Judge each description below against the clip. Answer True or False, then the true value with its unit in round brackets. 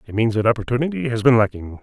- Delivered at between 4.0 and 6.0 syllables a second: False (7.1 syllables/s)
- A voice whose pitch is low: True (115 Hz)